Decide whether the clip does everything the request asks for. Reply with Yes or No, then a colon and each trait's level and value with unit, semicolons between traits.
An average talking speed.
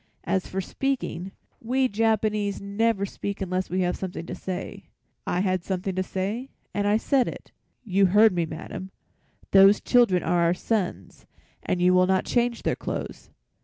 Yes: average, 165 wpm